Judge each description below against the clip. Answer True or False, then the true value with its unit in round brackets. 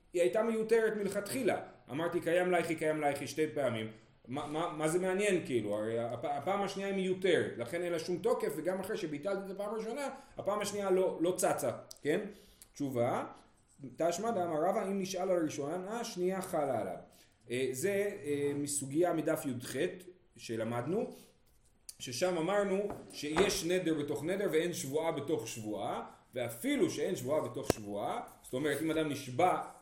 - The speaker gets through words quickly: True (155 wpm)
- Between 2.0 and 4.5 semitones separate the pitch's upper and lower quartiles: False (5.2 semitones)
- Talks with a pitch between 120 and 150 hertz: False (170 Hz)